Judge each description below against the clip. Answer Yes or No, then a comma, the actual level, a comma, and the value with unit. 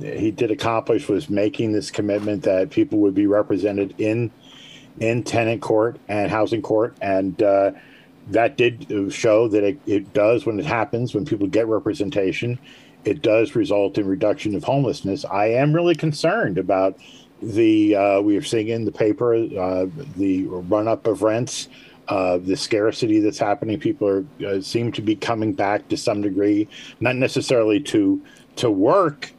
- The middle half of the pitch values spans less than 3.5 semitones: Yes, average, 3.1 semitones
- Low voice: Yes, low, 110 Hz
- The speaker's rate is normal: Yes, average, 165 wpm